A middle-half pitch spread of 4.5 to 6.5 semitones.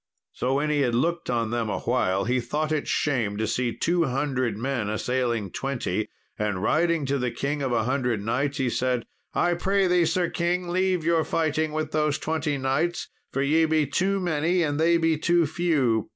Yes: average, 5.1 semitones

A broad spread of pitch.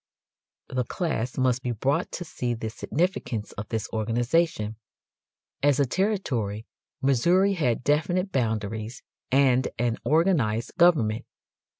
Yes: wide, 6.2 semitones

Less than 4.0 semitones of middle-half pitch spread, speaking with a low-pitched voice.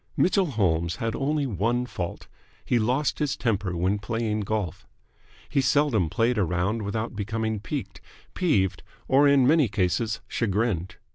No: average, 5.0 semitones; low, 110 Hz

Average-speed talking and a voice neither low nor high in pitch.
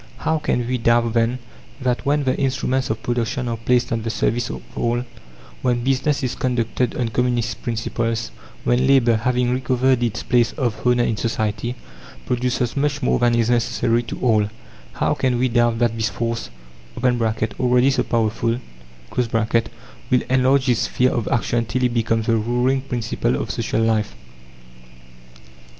No: average, 160 wpm; low, 120 Hz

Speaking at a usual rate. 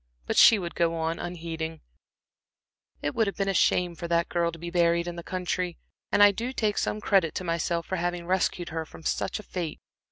No: fast, 220 wpm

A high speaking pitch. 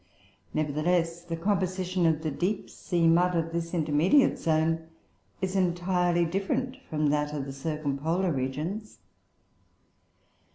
No: medium, 170 Hz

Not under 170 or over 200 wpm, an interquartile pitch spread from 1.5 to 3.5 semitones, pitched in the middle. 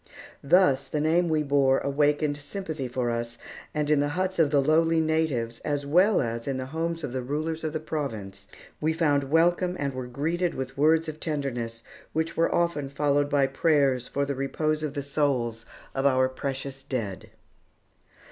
Yes: average, 180 wpm; average, 3.1 semitones; medium, 145 Hz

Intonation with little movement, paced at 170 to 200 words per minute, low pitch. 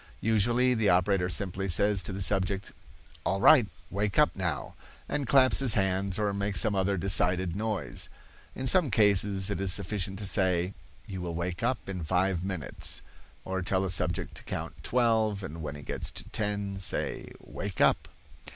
Yes: narrow, 2.2 semitones; average, 175 wpm; very low, 95 Hz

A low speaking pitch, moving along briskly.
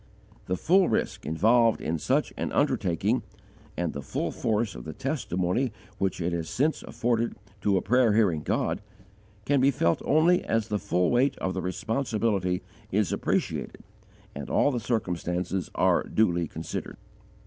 No: low, 105 Hz; average, 155 wpm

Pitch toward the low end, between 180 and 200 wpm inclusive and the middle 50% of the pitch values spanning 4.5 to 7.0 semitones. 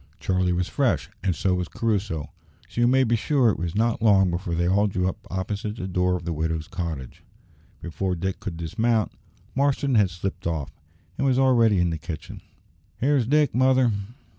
Yes: very low, 95 Hz; average, 190 wpm; average, 5.1 semitones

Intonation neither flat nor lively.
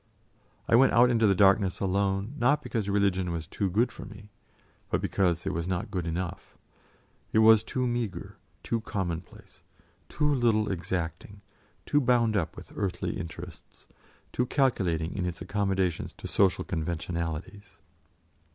Yes: average, 4.1 semitones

